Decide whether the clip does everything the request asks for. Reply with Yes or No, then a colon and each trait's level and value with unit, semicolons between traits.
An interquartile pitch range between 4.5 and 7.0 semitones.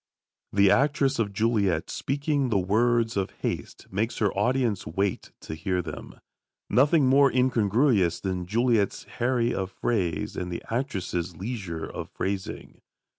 Yes: average, 5.1 semitones